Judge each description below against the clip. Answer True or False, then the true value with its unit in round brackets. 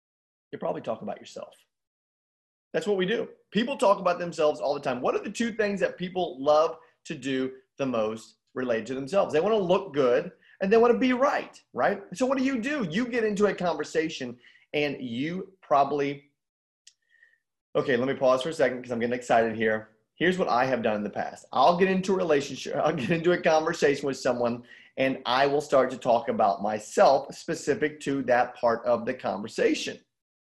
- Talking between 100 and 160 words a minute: False (200 wpm)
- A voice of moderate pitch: True (155 Hz)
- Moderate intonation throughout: False (7.8 semitones)